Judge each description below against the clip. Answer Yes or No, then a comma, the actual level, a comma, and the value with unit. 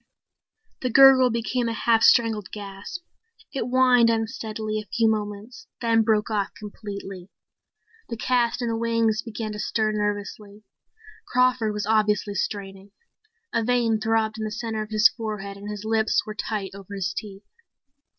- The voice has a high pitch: Yes, high, 220 Hz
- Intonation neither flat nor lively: No, narrow, 1.8 semitones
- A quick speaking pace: No, average, 155 wpm